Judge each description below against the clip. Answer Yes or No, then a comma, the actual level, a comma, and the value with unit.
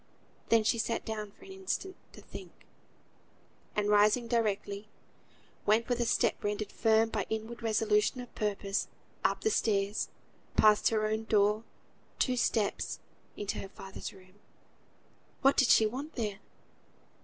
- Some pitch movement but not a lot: No, narrow, 2.0 semitones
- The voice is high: Yes, high, 215 Hz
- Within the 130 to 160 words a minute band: Yes, average, 145 wpm